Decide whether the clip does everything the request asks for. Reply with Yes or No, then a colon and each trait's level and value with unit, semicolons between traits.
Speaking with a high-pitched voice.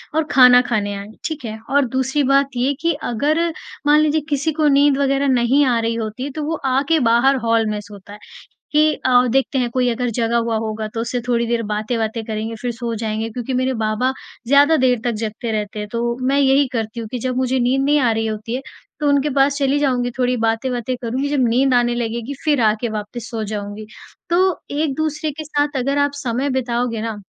Yes: high, 245 Hz